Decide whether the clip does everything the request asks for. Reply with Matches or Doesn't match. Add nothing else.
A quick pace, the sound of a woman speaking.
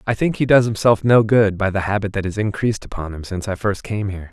Doesn't match